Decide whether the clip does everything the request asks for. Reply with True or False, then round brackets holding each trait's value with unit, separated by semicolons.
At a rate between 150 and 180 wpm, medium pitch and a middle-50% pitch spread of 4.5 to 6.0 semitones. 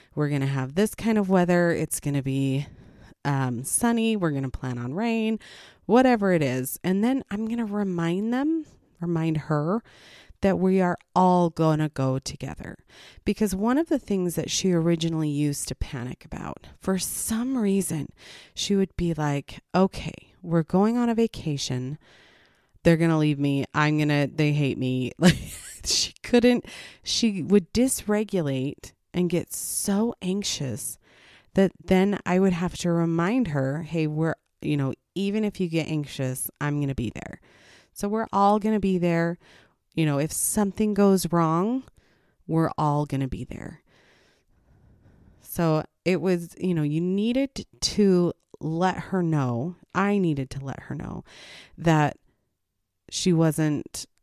True (160 wpm; 170 Hz; 5.5 semitones)